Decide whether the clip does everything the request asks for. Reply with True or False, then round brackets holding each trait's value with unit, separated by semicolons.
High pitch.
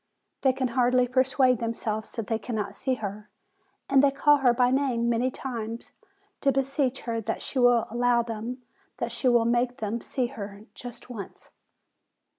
True (245 Hz)